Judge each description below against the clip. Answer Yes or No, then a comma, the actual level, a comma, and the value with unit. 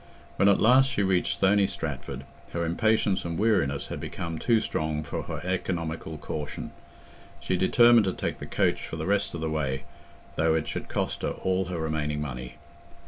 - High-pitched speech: No, very low, 85 Hz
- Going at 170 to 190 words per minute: Yes, average, 185 wpm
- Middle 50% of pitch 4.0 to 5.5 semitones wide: Yes, average, 4.3 semitones